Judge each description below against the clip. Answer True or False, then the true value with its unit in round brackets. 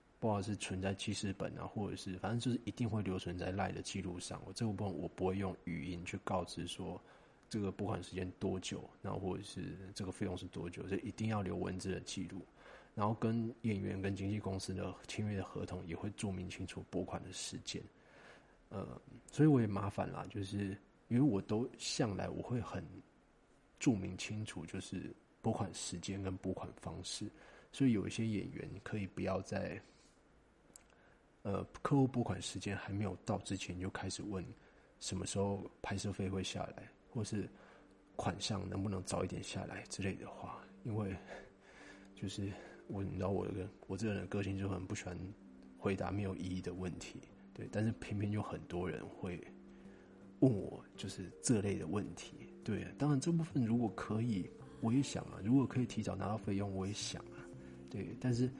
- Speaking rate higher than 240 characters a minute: True (275 characters per minute)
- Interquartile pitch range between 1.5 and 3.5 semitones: True (2.5 semitones)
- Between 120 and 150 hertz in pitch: False (100 Hz)